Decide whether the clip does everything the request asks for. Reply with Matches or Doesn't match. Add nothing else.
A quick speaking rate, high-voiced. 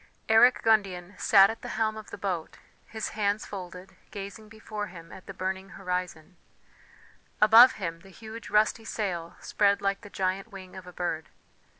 Doesn't match